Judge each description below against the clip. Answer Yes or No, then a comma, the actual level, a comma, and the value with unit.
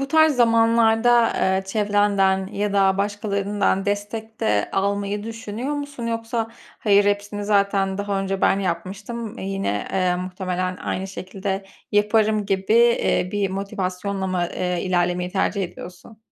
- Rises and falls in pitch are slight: Yes, narrow, 2.3 semitones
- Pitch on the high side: Yes, high, 200 Hz